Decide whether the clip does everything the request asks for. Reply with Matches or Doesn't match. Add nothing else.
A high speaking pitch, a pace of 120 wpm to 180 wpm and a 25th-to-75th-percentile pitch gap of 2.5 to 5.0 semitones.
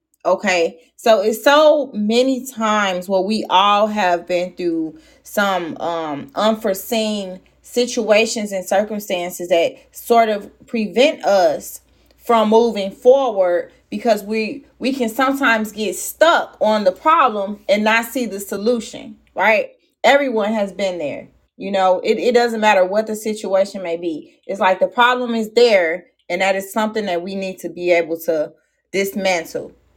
Matches